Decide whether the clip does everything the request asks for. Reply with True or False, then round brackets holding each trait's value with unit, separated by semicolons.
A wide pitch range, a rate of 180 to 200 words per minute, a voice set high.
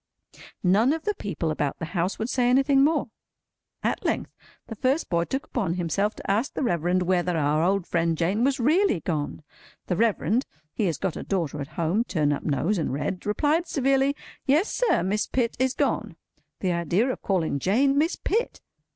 True (7.8 semitones; 185 wpm; 200 Hz)